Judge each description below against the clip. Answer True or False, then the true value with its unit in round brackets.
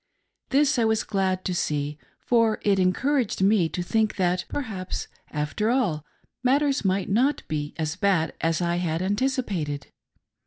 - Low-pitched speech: False (195 Hz)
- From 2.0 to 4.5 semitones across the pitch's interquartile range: False (5.2 semitones)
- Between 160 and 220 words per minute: False (150 wpm)